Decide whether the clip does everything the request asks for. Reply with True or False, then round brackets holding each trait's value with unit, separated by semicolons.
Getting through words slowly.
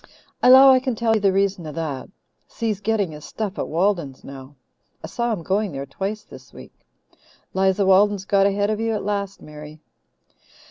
False (190 wpm)